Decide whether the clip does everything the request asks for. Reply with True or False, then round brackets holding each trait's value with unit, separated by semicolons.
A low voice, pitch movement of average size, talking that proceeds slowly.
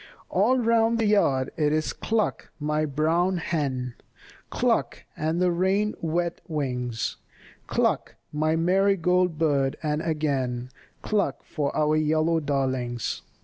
False (155 Hz; 4.3 semitones; 120 wpm)